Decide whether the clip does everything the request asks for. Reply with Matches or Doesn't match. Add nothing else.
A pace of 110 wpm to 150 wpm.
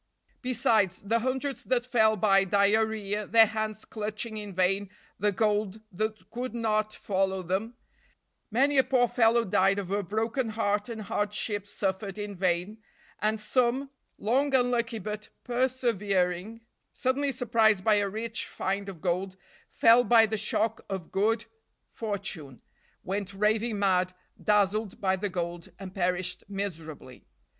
Matches